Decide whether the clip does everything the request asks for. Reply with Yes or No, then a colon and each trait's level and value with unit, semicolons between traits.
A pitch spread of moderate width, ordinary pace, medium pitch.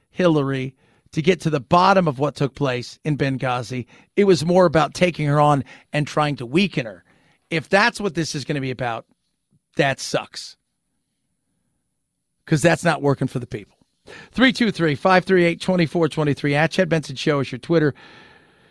Yes: average, 4.2 semitones; average, 190 wpm; medium, 155 Hz